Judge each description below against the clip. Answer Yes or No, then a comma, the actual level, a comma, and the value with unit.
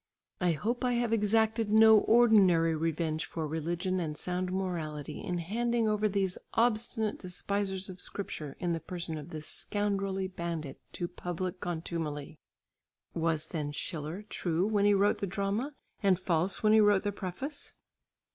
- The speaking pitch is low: No, medium, 185 Hz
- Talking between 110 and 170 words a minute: Yes, average, 155 wpm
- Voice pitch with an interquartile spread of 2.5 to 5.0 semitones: Yes, average, 4.1 semitones